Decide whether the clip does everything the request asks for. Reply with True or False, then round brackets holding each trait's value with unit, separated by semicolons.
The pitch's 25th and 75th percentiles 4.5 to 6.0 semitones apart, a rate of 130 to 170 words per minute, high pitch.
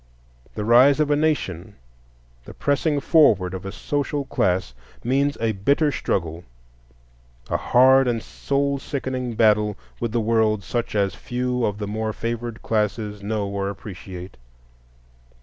False (4.8 semitones; 140 wpm; 115 Hz)